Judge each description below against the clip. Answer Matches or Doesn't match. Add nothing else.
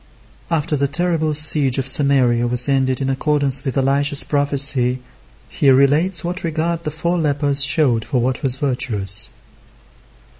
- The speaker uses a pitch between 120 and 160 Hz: Matches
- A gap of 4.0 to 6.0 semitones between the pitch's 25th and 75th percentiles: Doesn't match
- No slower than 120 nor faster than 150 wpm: Matches